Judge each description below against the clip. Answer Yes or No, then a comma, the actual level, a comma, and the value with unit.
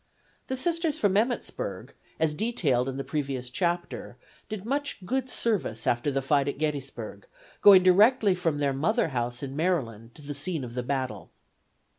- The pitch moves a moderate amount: No, wide, 7.6 semitones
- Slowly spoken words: No, average, 165 wpm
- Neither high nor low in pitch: Yes, medium, 150 Hz